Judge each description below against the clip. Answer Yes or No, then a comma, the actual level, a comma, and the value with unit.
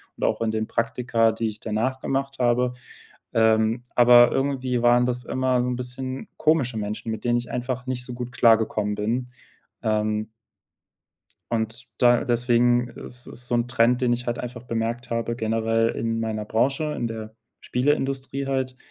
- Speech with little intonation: Yes, narrow, 1.8 semitones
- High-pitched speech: No, low, 120 Hz